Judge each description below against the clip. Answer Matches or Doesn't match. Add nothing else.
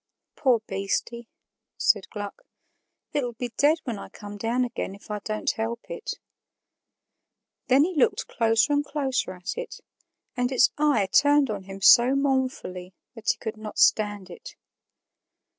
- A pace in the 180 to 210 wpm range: Doesn't match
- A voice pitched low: Doesn't match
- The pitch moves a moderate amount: Matches